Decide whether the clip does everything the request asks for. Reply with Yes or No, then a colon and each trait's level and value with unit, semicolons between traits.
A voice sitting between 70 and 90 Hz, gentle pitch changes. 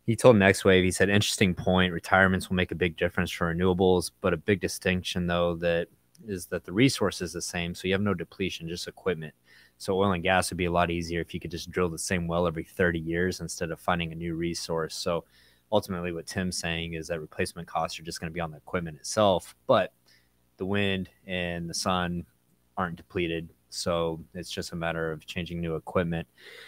Yes: very low, 85 Hz; narrow, 1.9 semitones